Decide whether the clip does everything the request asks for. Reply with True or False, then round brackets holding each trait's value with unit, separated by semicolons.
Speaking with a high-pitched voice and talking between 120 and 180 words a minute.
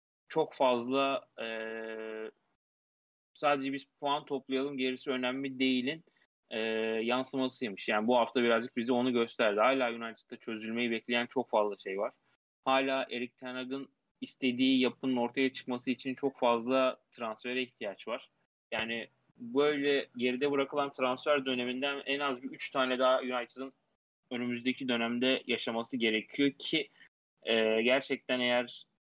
False (130 Hz; 130 wpm)